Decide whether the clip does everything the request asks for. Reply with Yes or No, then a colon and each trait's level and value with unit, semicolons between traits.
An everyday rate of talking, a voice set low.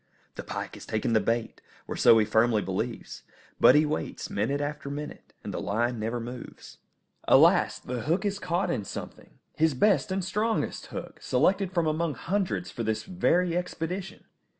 No: average, 175 wpm; medium, 150 Hz